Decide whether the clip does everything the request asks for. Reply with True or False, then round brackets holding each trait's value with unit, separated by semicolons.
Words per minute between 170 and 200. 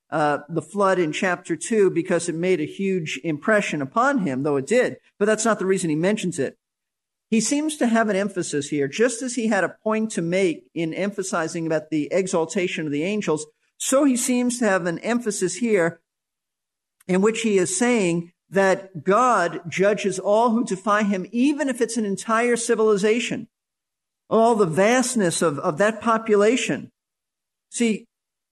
True (175 wpm)